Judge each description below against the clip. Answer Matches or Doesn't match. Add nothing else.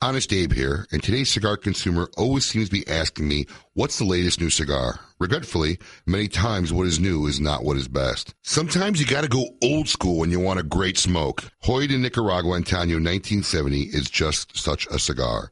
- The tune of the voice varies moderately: Doesn't match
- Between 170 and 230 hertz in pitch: Doesn't match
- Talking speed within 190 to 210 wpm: Matches